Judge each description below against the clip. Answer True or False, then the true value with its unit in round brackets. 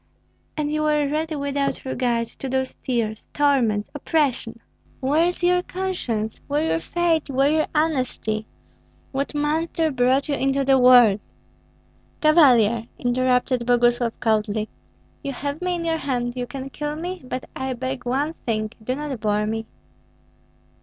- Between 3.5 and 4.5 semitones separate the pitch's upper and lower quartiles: True (3.9 semitones)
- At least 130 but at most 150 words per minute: True (145 wpm)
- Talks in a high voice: True (265 Hz)